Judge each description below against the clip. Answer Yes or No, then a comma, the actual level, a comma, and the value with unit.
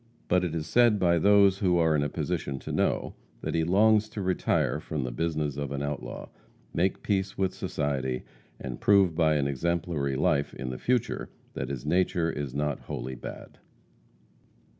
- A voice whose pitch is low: Yes, very low, 80 Hz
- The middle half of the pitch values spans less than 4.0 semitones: No, average, 4.8 semitones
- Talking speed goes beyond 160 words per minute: Yes, average, 180 wpm